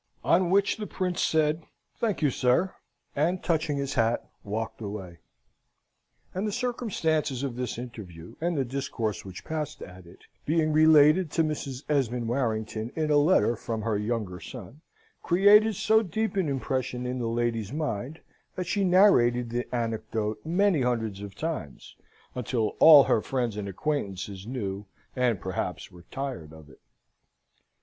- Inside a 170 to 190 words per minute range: No, average, 155 wpm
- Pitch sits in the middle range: No, low, 125 Hz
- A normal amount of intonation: No, wide, 6.5 semitones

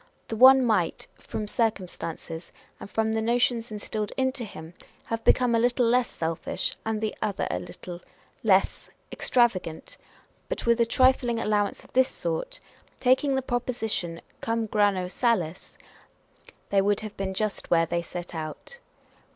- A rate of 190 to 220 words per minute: No, average, 150 wpm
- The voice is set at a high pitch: Yes, high, 220 Hz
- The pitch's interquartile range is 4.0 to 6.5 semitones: Yes, average, 4.5 semitones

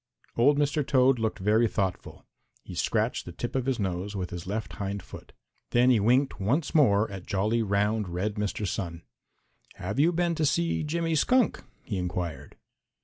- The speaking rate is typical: Yes, average, 175 wpm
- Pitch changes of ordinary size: No, wide, 6.1 semitones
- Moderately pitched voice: No, low, 110 Hz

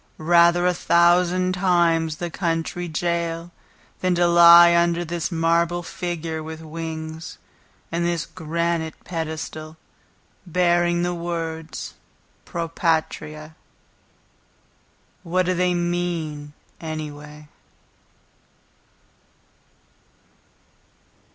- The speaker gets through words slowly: Yes, slow, 85 wpm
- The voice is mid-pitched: Yes, medium, 170 Hz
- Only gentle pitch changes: Yes, narrow, 1.4 semitones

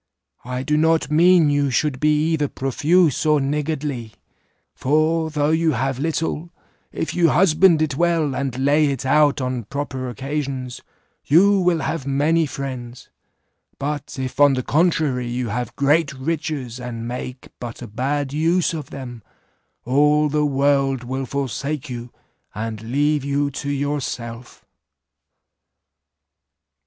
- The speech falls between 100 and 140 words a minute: Yes, slow, 135 wpm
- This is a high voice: No, medium, 140 Hz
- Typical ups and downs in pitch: Yes, average, 3.1 semitones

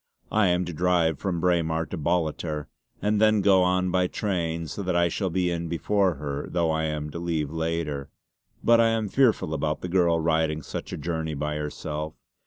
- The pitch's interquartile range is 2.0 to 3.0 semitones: Yes, average, 2.7 semitones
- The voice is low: Yes, very low, 85 Hz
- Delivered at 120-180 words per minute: No, average, 195 wpm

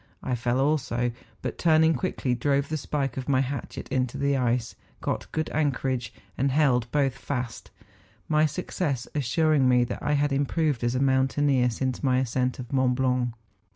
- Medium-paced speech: Yes, average, 170 wpm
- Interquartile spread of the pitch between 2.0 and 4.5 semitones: Yes, narrow, 2.6 semitones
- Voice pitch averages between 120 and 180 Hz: Yes, low, 135 Hz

